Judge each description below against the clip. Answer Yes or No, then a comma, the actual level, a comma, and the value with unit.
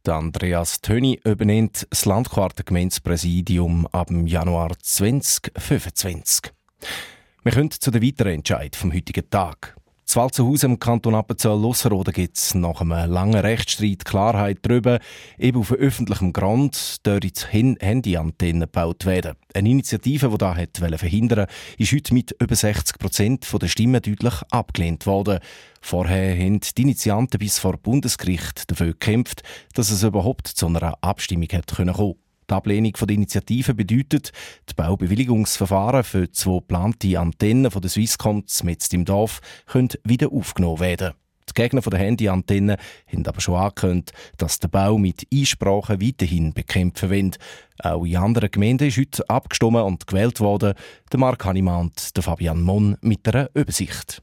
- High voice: No, low, 100 Hz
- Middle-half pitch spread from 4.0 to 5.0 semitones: Yes, average, 4.6 semitones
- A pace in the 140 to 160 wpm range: Yes, average, 145 wpm